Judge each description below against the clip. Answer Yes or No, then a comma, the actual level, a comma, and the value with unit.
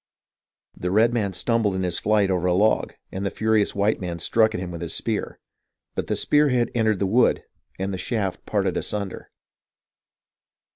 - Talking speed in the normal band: Yes, average, 180 wpm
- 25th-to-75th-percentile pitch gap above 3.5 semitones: No, average, 3.0 semitones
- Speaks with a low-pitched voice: Yes, low, 100 Hz